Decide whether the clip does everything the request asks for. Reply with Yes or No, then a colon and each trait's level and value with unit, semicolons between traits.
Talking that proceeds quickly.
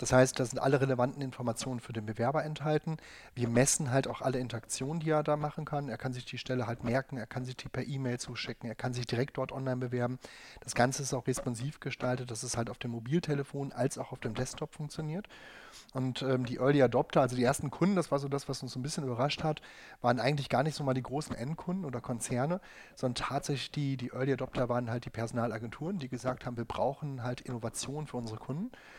Yes: fast, 230 wpm